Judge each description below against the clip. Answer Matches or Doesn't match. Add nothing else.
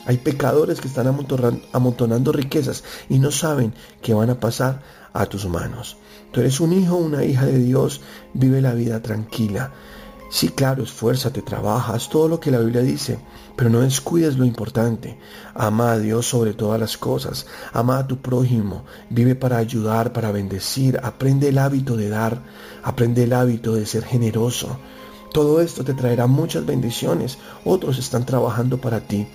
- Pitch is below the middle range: Matches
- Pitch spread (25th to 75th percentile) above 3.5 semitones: Doesn't match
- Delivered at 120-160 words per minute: Doesn't match